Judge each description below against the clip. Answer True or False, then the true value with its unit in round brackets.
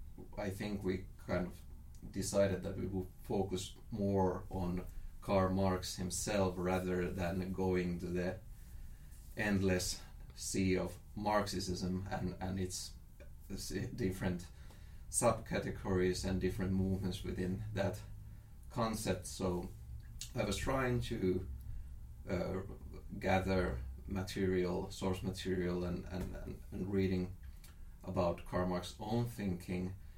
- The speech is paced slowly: True (105 wpm)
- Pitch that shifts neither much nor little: False (1.4 semitones)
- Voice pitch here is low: True (95 Hz)